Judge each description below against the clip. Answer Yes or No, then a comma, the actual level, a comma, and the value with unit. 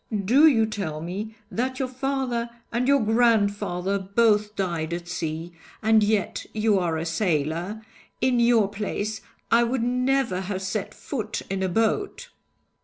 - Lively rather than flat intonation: No, average, 4.2 semitones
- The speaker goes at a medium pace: Yes, average, 150 wpm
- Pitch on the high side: Yes, high, 215 Hz